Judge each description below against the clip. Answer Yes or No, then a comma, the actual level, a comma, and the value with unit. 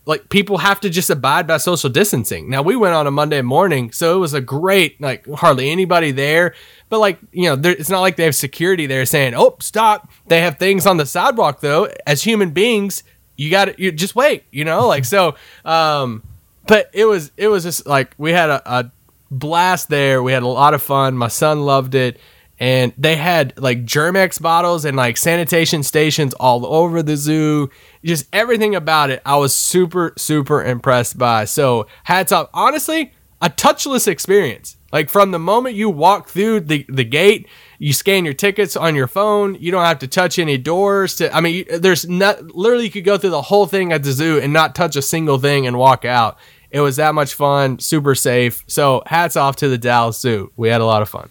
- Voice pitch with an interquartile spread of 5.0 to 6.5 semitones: Yes, wide, 5.5 semitones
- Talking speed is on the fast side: Yes, fast, 215 wpm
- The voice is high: No, medium, 160 Hz